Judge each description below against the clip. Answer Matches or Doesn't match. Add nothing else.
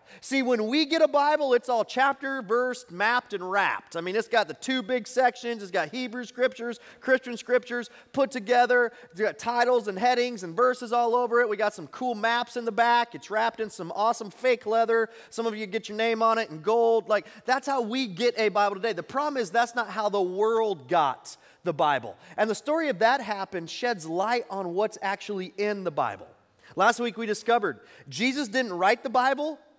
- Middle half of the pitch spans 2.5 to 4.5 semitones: Matches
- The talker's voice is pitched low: Doesn't match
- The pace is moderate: Doesn't match